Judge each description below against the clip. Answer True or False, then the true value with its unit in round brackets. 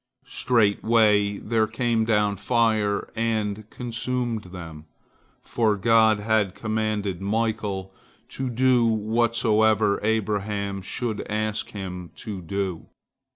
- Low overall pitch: True (110 Hz)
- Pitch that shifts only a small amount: True (2.1 semitones)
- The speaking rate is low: True (100 wpm)